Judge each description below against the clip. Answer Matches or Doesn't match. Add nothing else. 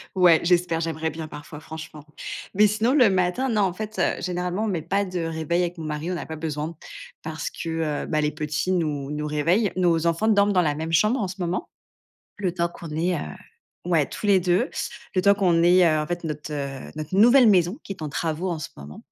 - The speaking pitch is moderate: Matches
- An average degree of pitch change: Matches